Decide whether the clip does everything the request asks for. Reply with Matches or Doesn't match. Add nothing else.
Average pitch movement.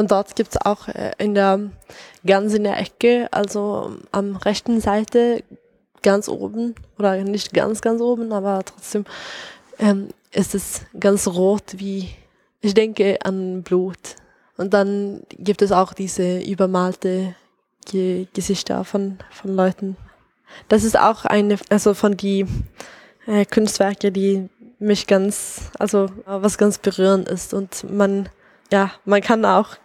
Doesn't match